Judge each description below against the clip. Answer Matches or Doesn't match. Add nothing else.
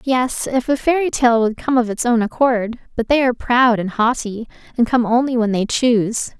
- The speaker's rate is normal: Doesn't match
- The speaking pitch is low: Doesn't match